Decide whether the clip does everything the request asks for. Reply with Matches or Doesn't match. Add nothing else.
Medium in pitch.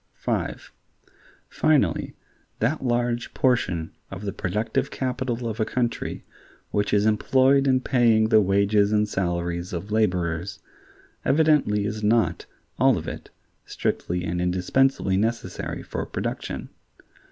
Doesn't match